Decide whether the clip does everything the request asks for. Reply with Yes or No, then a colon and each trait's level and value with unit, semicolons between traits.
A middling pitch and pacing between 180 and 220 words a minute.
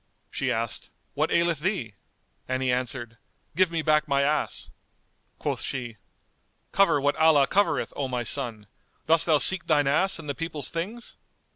No: medium, 150 Hz; average, 160 wpm